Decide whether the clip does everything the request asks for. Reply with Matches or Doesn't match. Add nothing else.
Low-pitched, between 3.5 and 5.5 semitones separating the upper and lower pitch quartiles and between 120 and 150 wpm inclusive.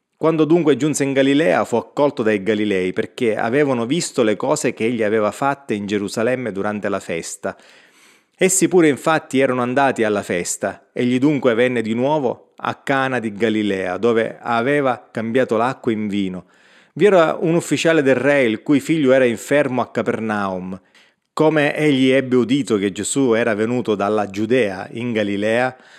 Doesn't match